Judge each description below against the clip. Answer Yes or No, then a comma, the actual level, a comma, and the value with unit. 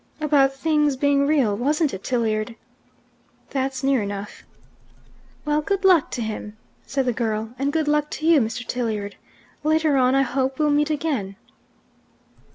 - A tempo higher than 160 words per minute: No, average, 155 wpm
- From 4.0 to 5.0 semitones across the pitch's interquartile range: Yes, average, 4.6 semitones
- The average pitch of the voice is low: No, very high, 270 Hz